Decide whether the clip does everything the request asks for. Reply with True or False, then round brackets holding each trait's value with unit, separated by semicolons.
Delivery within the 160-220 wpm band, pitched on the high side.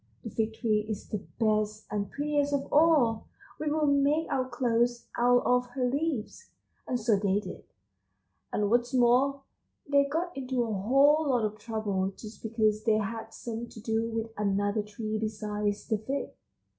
True (170 wpm; 230 Hz)